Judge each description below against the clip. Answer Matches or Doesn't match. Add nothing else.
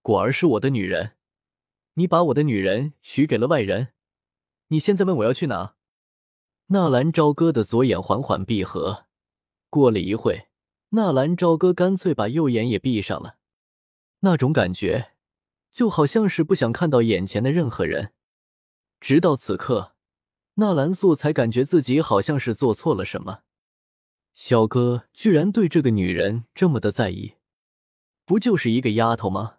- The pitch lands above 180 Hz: Doesn't match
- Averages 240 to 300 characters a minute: Doesn't match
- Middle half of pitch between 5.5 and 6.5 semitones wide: Doesn't match